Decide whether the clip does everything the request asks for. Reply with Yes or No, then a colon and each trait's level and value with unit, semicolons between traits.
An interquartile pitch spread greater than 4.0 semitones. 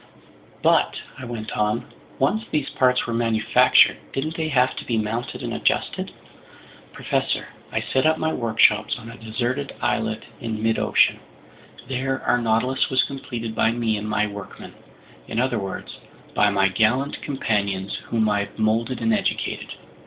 No: average, 3.2 semitones